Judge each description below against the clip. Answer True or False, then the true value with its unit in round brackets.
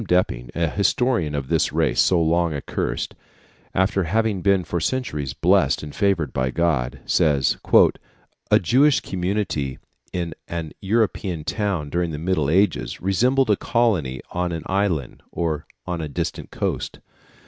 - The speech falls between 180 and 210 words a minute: False (145 wpm)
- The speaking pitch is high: False (85 Hz)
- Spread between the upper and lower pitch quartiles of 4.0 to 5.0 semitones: True (4.6 semitones)